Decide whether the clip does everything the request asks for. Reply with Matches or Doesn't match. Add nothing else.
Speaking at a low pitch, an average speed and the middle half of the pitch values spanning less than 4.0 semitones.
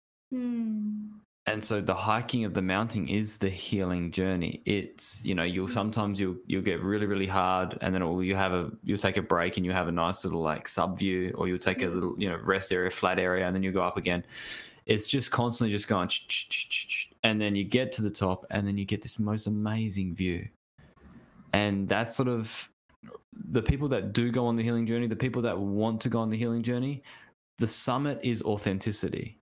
Doesn't match